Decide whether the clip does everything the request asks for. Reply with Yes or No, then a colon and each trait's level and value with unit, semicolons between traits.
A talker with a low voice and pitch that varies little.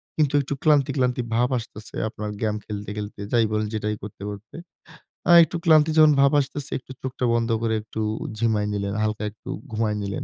No: low, 110 Hz; average, 4.0 semitones